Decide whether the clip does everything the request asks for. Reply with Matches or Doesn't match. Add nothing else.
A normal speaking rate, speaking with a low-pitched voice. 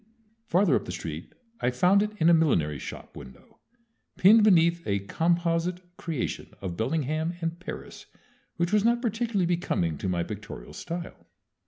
Doesn't match